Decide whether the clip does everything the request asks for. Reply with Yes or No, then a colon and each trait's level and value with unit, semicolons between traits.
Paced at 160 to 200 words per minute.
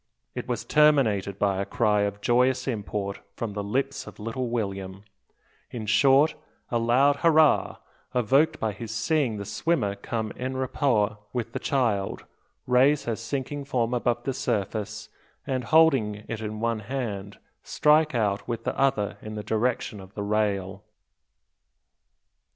No: average, 150 wpm